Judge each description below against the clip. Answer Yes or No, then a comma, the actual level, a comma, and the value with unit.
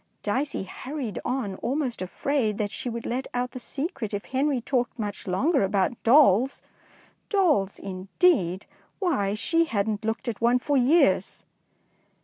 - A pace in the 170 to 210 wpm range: No, average, 145 wpm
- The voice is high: Yes, high, 240 Hz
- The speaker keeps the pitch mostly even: No, average, 5.3 semitones